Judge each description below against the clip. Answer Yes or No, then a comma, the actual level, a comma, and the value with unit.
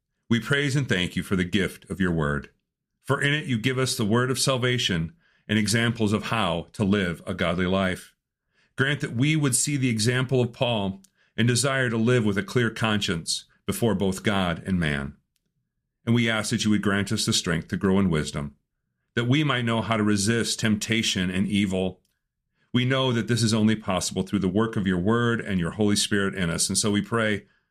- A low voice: Yes, low, 110 Hz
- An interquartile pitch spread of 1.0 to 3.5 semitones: No, average, 3.9 semitones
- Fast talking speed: Yes, fast, 215 wpm